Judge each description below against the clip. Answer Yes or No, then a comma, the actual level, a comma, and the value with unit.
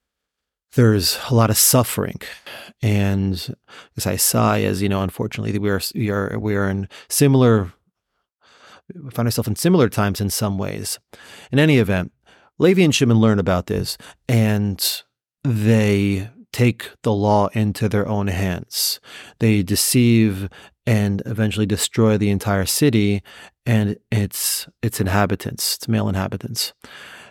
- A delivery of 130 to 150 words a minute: Yes, average, 140 wpm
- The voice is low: Yes, low, 105 Hz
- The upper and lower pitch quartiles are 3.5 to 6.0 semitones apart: No, narrow, 2.5 semitones